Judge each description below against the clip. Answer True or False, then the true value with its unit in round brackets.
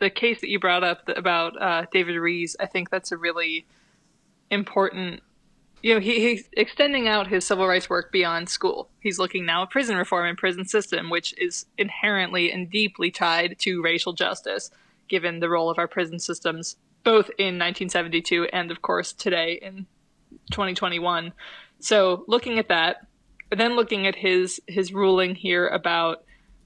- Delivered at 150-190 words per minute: True (170 wpm)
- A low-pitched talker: False (185 Hz)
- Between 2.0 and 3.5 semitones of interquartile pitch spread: True (2.9 semitones)